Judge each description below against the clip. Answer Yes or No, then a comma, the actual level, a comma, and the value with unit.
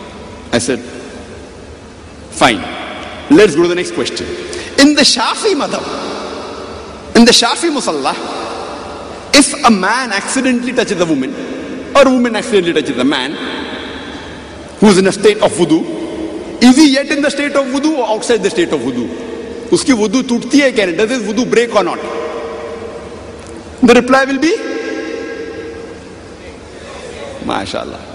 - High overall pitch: Yes, high, 245 Hz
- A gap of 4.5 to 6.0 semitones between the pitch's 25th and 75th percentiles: Yes, average, 5.2 semitones